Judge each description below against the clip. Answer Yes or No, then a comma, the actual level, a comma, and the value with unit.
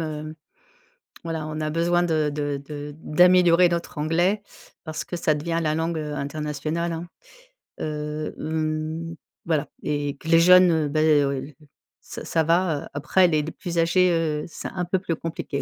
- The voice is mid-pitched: Yes, medium, 160 Hz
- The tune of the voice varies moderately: No, narrow, 2.0 semitones